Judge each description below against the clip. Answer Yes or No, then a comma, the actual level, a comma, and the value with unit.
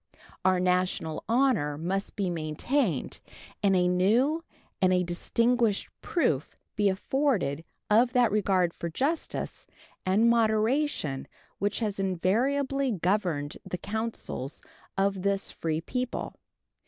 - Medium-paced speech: No, slow, 115 wpm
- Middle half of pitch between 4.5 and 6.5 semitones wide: Yes, average, 4.8 semitones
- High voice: Yes, high, 195 Hz